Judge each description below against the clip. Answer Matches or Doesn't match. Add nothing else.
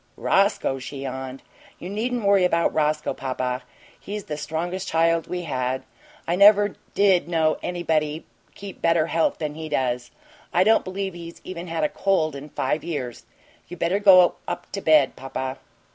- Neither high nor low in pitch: Matches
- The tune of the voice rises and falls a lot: Doesn't match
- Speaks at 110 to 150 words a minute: Doesn't match